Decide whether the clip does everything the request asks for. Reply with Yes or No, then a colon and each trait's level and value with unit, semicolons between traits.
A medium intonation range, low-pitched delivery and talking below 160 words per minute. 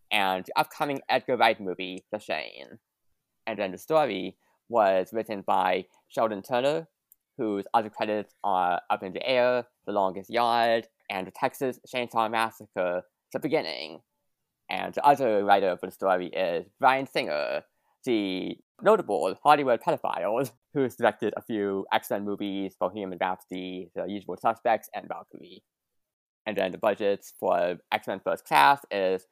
Yes: average, 3.7 semitones; low, 105 Hz; average, 150 wpm